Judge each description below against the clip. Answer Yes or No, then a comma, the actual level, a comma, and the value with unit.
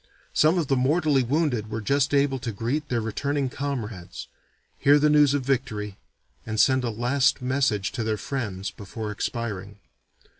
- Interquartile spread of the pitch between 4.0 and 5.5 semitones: Yes, average, 4.5 semitones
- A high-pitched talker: No, low, 130 Hz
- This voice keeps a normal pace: Yes, average, 160 wpm